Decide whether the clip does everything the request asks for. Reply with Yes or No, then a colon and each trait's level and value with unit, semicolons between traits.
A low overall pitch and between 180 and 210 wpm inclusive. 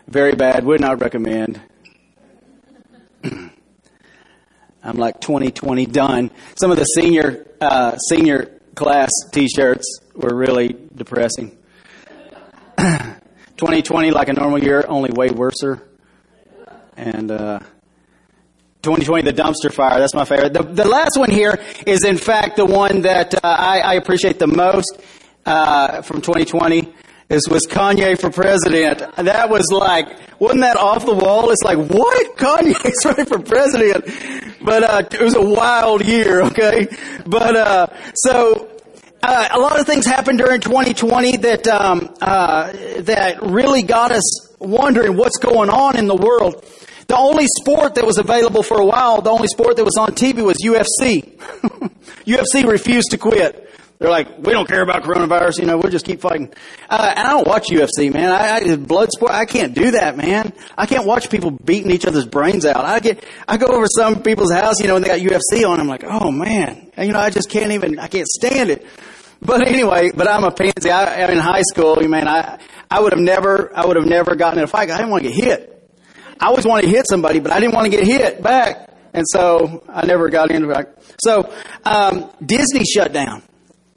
No: high, 190 Hz; average, 185 wpm